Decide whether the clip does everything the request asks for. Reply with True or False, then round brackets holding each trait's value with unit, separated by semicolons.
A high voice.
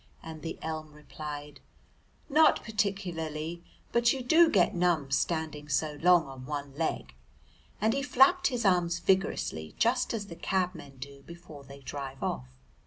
False (165 Hz)